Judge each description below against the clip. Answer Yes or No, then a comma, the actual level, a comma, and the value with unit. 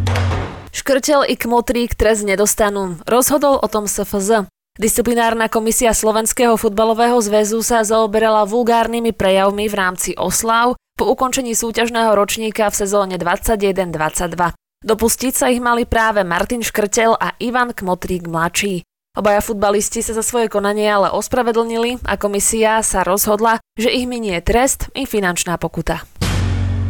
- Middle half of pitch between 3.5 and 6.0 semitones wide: No, average, 2.9 semitones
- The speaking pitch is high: Yes, high, 220 Hz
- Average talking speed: Yes, average, 130 wpm